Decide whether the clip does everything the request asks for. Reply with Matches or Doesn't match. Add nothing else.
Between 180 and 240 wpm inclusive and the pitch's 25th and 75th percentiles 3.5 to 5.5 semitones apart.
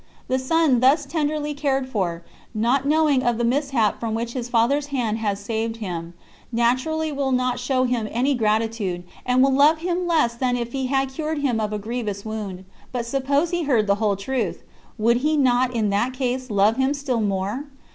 Matches